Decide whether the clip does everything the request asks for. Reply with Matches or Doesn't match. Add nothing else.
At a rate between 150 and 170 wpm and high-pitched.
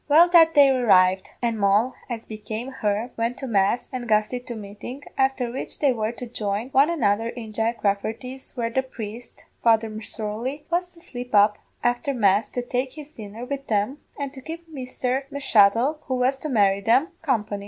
Doesn't match